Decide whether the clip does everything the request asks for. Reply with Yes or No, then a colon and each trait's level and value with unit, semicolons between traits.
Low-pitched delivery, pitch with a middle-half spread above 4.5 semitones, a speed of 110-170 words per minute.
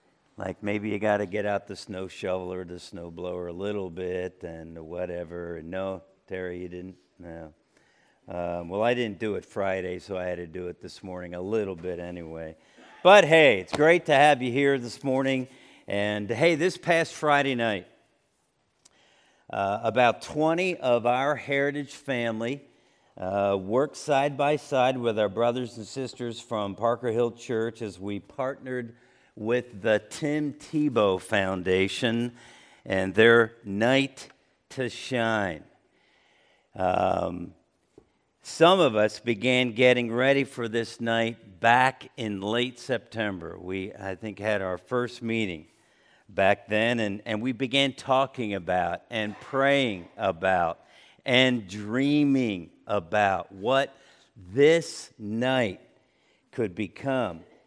Yes: low, 115 Hz; wide, 5.4 semitones; average, 140 wpm